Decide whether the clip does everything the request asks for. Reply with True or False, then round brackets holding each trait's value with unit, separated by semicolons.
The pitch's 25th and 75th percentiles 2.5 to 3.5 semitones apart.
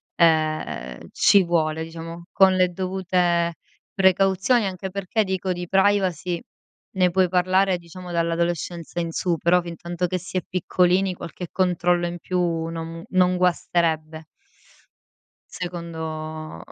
False (1.8 semitones)